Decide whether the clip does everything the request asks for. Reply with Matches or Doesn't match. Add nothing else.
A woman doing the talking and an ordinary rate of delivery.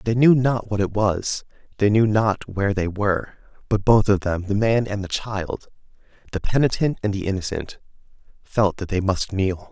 Doesn't match